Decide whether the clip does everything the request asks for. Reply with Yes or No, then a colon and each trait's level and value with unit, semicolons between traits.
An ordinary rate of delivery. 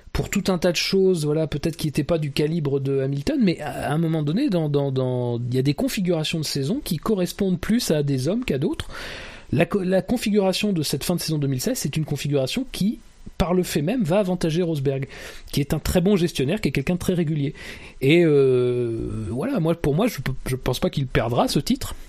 No: fast, 230 wpm